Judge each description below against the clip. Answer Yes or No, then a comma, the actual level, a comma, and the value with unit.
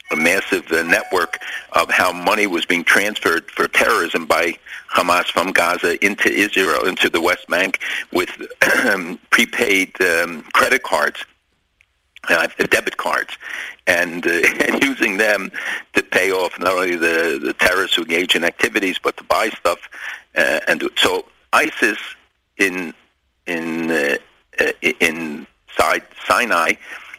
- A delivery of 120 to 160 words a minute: Yes, slow, 135 wpm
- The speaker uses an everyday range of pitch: No, wide, 8.4 semitones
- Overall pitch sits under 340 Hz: No, very high, 360 Hz